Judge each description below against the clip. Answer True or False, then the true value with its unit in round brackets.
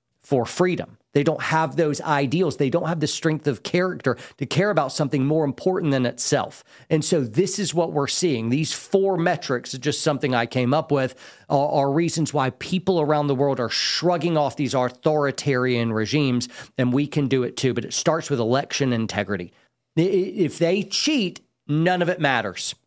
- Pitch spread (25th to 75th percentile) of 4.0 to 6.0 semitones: True (4.4 semitones)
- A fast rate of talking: False (185 wpm)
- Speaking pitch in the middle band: True (150 Hz)